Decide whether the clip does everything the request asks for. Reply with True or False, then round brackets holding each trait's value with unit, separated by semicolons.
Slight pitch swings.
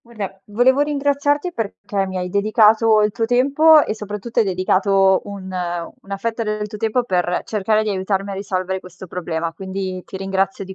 False (3.0 semitones)